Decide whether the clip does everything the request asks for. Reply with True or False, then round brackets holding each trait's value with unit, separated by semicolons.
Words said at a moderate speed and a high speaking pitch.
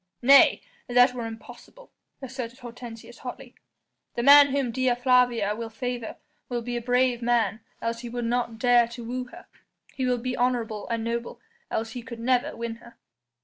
True (175 wpm; 240 Hz)